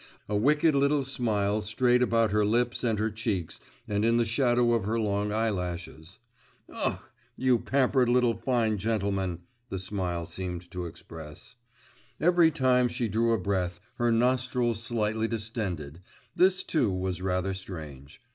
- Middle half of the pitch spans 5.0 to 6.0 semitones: No, average, 4.5 semitones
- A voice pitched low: Yes, low, 110 Hz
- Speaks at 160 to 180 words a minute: No, average, 145 wpm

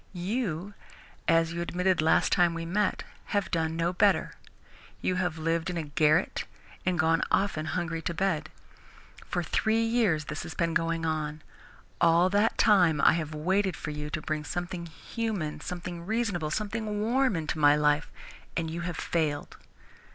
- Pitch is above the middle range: No, medium, 170 Hz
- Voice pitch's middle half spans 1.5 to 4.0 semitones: Yes, average, 3.3 semitones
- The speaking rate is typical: Yes, average, 165 wpm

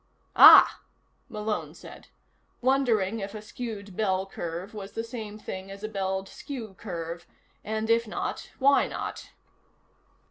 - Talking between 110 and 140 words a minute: Yes, slow, 135 wpm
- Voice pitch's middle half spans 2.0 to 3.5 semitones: Yes, average, 2.8 semitones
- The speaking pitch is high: Yes, high, 210 Hz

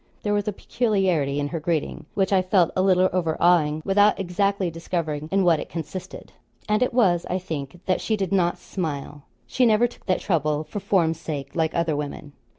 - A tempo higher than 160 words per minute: Yes, average, 195 wpm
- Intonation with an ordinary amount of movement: Yes, average, 3.8 semitones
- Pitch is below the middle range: No, medium, 175 Hz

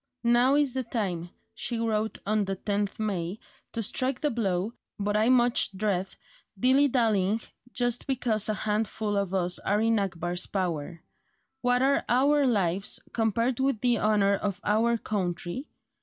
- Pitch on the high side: Yes, high, 215 Hz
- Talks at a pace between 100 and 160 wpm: Yes, average, 155 wpm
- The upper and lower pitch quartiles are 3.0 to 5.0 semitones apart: Yes, average, 3.8 semitones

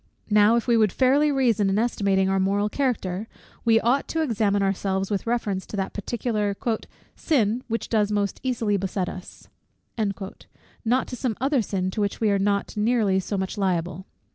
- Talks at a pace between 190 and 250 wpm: No, average, 175 wpm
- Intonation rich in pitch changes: No, average, 3.3 semitones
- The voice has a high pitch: Yes, high, 210 Hz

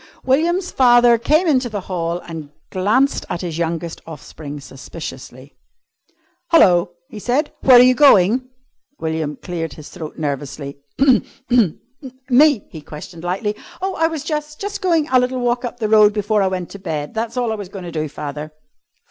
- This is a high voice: Yes, high, 205 Hz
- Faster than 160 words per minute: Yes, average, 170 wpm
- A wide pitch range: Yes, wide, 7.7 semitones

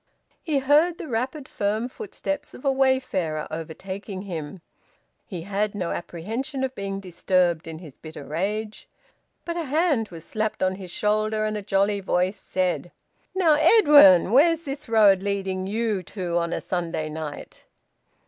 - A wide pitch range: Yes, wide, 6.5 semitones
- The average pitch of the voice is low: No, high, 200 Hz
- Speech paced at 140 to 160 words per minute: Yes, average, 155 wpm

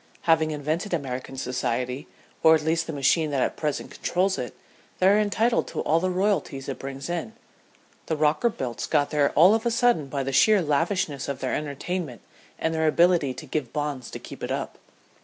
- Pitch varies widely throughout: No, average, 4.5 semitones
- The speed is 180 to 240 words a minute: Yes, average, 195 wpm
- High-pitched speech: No, medium, 155 Hz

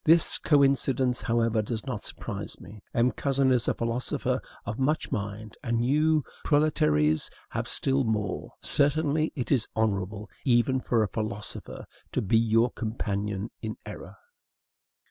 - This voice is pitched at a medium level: No, low, 115 Hz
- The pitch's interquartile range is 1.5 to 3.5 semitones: No, average, 4.0 semitones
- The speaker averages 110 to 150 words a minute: Yes, average, 140 wpm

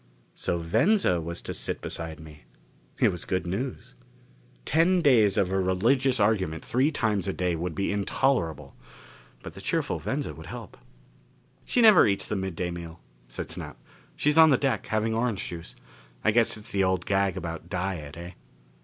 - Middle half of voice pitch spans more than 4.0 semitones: Yes, wide, 5.6 semitones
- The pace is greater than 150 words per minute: Yes, average, 170 wpm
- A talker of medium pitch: No, very low, 95 Hz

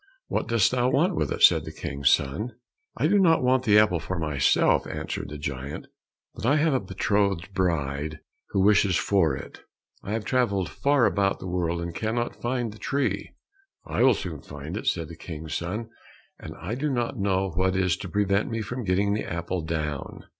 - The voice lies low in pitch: Yes, very low, 95 Hz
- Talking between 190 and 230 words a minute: Yes, average, 195 wpm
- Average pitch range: No, wide, 5.9 semitones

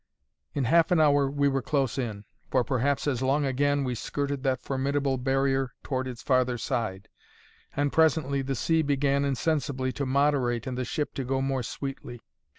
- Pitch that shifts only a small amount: Yes, narrow, 1.8 semitones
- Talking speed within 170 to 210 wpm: Yes, average, 175 wpm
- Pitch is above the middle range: No, low, 135 Hz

